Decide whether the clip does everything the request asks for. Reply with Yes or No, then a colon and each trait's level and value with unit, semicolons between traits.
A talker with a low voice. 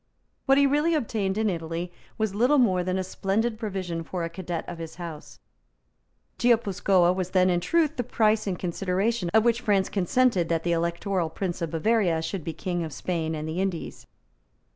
No: medium, 185 Hz